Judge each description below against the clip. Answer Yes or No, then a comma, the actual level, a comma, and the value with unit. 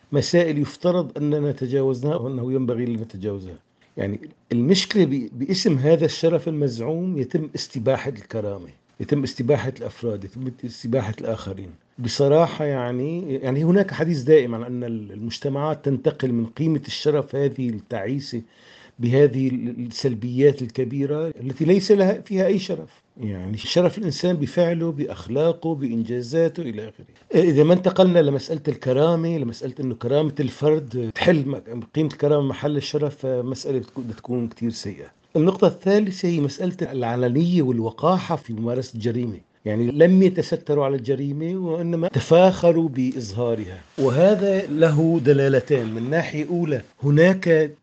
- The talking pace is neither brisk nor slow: Yes, average, 120 wpm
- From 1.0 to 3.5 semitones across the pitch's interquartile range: No, average, 5.2 semitones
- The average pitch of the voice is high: No, medium, 140 Hz